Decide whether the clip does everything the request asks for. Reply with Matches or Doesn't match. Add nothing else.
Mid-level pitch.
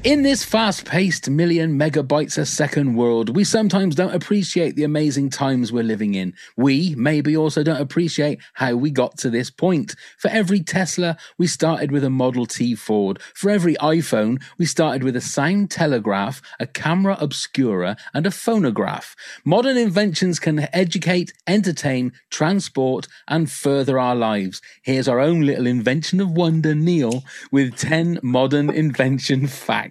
Matches